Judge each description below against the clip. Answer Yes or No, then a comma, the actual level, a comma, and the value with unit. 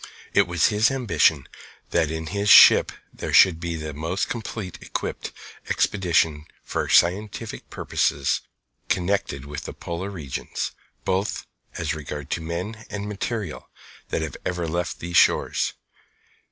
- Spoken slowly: Yes, slow, 125 wpm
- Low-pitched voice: Yes, very low, 85 Hz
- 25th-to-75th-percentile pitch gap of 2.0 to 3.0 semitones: No, average, 4.2 semitones